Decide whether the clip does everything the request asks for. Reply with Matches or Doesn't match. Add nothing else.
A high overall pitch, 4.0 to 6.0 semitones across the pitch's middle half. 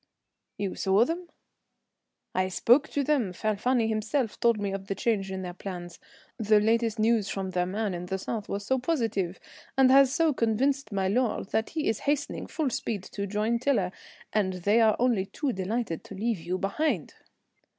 Matches